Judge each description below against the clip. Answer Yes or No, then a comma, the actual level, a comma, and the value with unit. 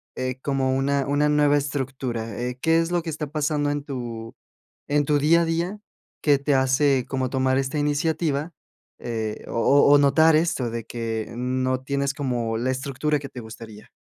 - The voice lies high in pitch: No, medium, 140 Hz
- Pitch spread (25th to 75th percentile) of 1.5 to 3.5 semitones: Yes, average, 2.7 semitones